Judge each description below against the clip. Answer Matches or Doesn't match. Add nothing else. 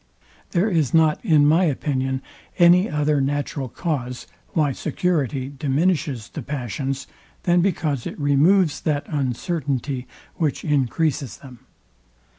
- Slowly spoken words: Matches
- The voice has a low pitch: Doesn't match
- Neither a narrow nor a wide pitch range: Matches